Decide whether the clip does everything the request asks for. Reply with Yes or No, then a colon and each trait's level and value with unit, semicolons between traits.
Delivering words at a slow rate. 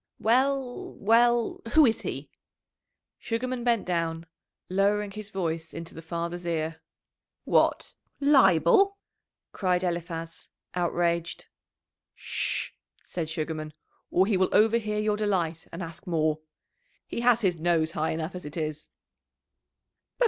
Yes: slow, 120 wpm